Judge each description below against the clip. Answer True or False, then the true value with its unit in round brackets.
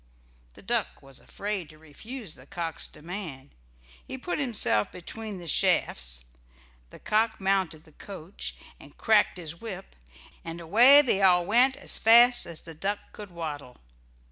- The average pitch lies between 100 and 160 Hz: False (180 Hz)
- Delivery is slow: False (150 wpm)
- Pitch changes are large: True (5.7 semitones)